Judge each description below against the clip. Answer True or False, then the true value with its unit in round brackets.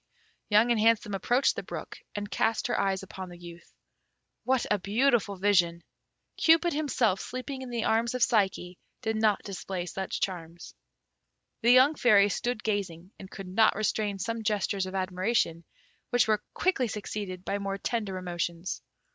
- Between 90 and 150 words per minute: False (160 wpm)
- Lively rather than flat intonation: False (3.7 semitones)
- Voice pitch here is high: True (205 Hz)